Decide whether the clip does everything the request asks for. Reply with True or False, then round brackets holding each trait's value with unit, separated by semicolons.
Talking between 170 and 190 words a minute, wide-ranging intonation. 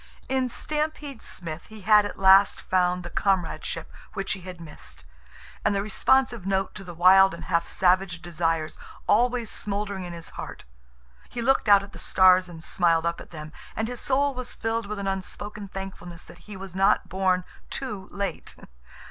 False (180 wpm; 3.2 semitones)